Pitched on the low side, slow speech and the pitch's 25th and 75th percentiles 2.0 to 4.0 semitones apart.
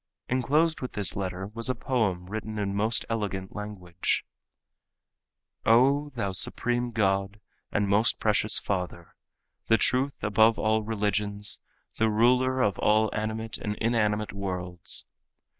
Yes: low, 105 Hz; slow, 125 wpm; narrow, 2.5 semitones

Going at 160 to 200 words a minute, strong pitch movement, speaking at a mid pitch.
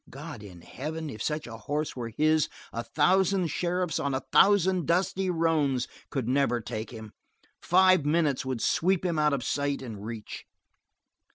Yes: average, 165 wpm; wide, 5.7 semitones; medium, 145 Hz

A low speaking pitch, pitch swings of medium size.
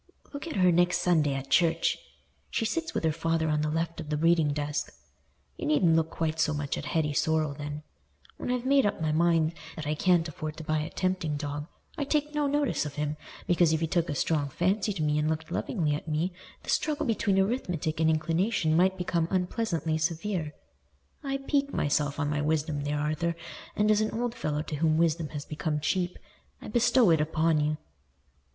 No: medium, 160 Hz; average, 3.5 semitones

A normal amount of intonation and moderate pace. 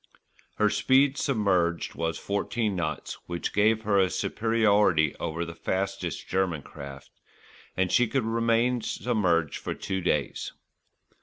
No: average, 5.0 semitones; slow, 130 wpm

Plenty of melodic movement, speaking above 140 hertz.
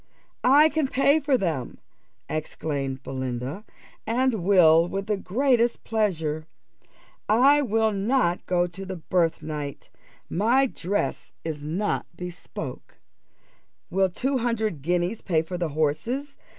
Yes: wide, 6.8 semitones; high, 190 Hz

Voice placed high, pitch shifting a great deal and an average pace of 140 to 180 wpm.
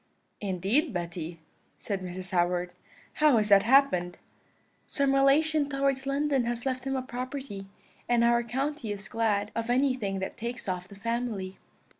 Yes: high, 235 Hz; wide, 5.8 semitones; average, 150 wpm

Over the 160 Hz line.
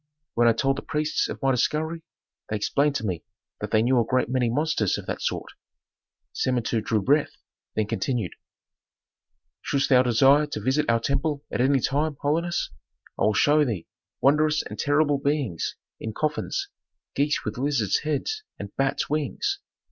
No: low, 135 Hz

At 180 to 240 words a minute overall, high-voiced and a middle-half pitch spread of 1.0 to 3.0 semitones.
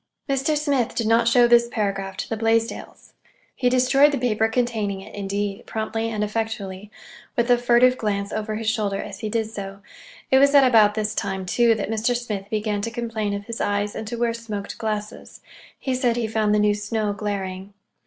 Yes: average, 195 wpm; high, 220 Hz; narrow, 2.5 semitones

